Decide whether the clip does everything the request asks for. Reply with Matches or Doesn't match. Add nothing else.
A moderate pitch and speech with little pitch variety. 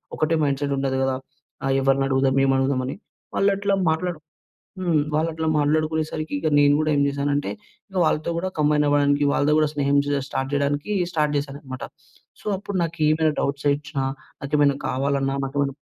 Matches